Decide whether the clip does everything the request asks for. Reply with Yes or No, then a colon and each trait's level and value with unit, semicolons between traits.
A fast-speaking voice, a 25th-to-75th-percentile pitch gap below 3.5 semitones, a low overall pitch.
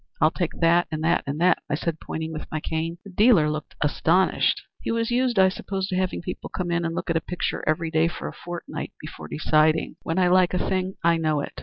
No: fast, 245 wpm; narrow, 2.6 semitones; medium, 170 Hz